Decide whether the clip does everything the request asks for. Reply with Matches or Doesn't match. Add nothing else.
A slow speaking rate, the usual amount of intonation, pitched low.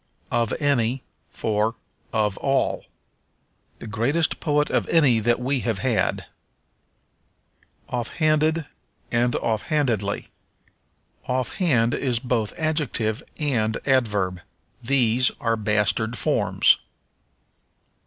Matches